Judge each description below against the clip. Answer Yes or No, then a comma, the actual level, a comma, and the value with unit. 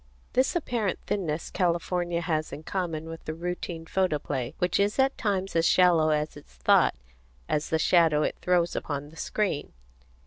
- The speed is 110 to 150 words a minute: No, average, 165 wpm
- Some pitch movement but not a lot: Yes, average, 3.1 semitones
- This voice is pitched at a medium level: Yes, medium, 170 Hz